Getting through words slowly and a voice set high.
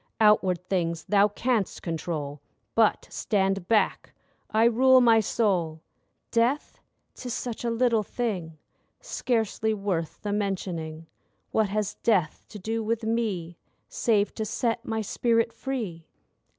Yes: slow, 125 wpm; high, 210 Hz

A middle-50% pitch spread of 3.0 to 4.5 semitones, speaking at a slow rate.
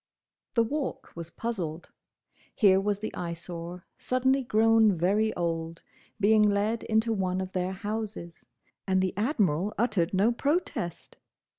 Yes: average, 4.1 semitones; slow, 130 wpm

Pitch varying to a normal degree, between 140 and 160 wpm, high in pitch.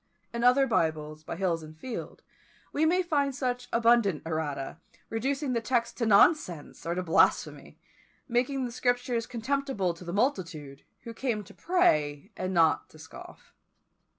No: wide, 7.6 semitones; average, 150 wpm; high, 230 Hz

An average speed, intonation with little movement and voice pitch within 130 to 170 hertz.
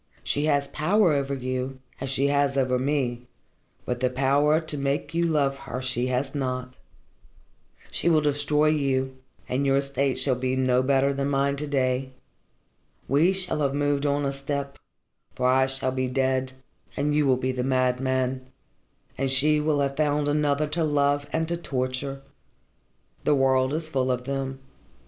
Yes: average, 170 wpm; narrow, 1.9 semitones; medium, 140 Hz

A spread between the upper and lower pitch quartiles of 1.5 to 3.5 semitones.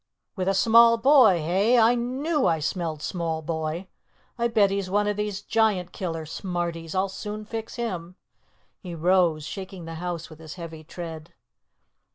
No: average, 4.5 semitones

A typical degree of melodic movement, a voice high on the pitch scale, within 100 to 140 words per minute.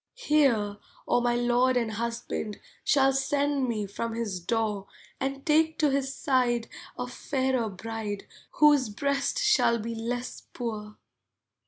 Yes: average, 3.5 semitones; high, 245 Hz; slow, 135 wpm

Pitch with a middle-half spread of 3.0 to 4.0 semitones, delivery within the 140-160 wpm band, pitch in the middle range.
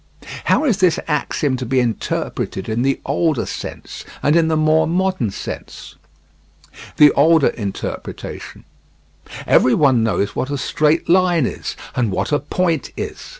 No: average, 4.6 semitones; average, 150 wpm; medium, 150 Hz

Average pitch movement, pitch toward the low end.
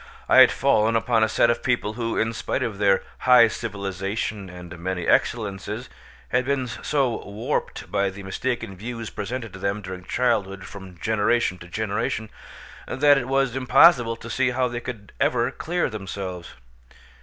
Yes: average, 3.9 semitones; low, 110 Hz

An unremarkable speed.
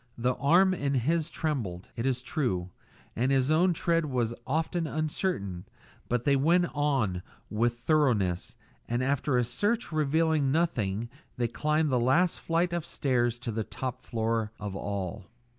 Yes: average, 155 wpm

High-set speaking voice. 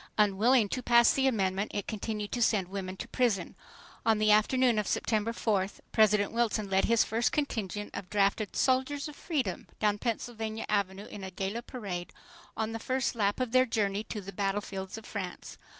Yes: high, 215 Hz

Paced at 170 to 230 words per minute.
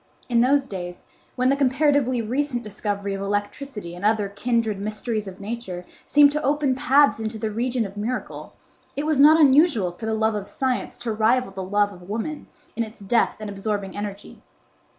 Yes: average, 185 wpm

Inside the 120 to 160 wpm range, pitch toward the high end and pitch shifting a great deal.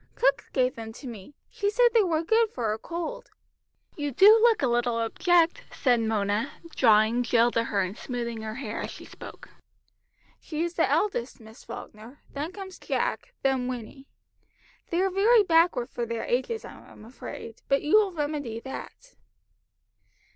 No: average, 170 wpm; very high, 265 Hz; wide, 7.3 semitones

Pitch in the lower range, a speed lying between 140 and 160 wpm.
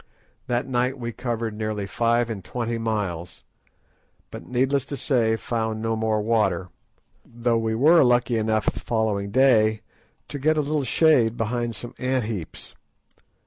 Yes: low, 115 Hz; average, 150 wpm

